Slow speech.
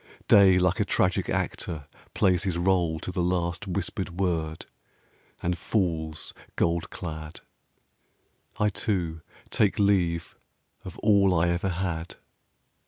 Yes: slow, 120 wpm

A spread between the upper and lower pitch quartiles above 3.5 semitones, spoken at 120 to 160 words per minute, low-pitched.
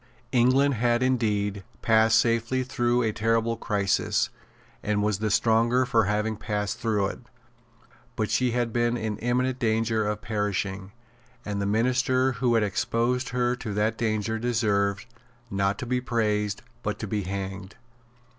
No: average, 2.7 semitones; average, 150 wpm; low, 110 Hz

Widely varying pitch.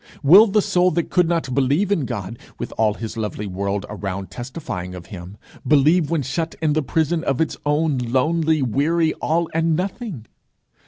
Yes: wide, 6.8 semitones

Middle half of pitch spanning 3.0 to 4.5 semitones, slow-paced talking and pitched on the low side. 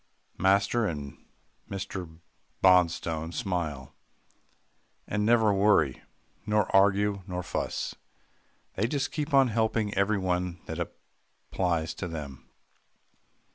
Yes: average, 3.9 semitones; slow, 95 wpm; very low, 95 Hz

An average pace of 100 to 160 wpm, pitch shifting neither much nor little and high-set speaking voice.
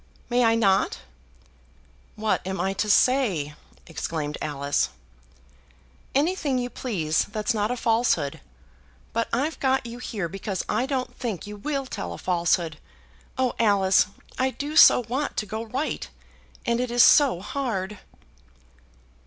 Yes: average, 140 wpm; average, 5.0 semitones; high, 225 Hz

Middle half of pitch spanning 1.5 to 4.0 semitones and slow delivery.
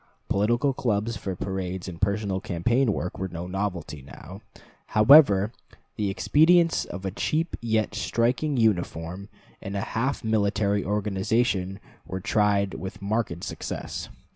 Yes: average, 3.2 semitones; slow, 130 wpm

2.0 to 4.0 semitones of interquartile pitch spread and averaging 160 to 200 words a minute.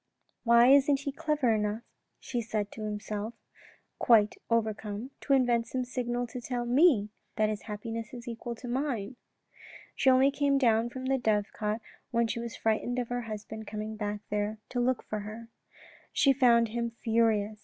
Yes: narrow, 2.6 semitones; average, 175 wpm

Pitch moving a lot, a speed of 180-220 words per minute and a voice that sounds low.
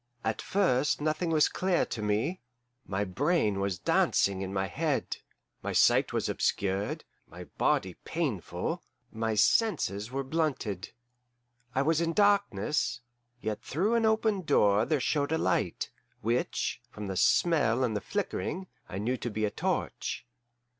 No: wide, 8.0 semitones; average, 145 wpm; low, 130 Hz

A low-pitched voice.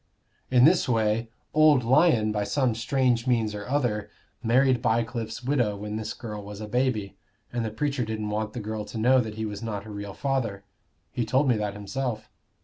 Yes: low, 115 Hz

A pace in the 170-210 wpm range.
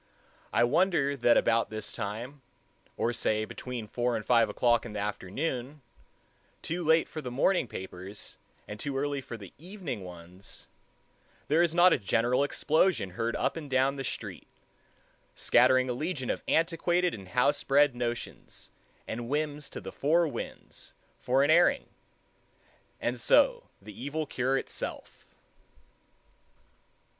No: average, 140 wpm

